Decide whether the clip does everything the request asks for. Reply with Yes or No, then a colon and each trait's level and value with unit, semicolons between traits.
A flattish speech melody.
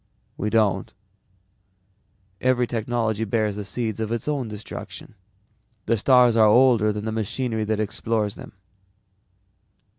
Yes: narrow, 2.2 semitones